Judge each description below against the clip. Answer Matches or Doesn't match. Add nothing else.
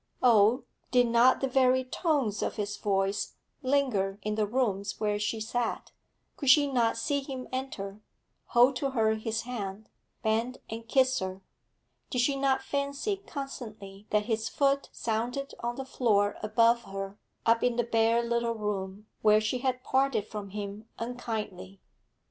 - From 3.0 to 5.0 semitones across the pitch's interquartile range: Matches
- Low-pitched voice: Doesn't match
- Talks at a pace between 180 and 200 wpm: Doesn't match